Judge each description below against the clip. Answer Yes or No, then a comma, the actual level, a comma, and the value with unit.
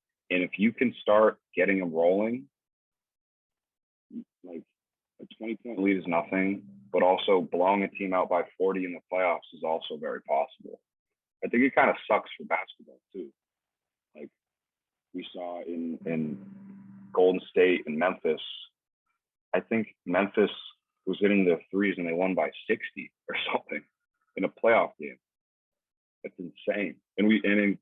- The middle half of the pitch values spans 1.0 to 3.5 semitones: Yes, average, 3.2 semitones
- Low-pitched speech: Yes, very low, 95 Hz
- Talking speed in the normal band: Yes, average, 155 wpm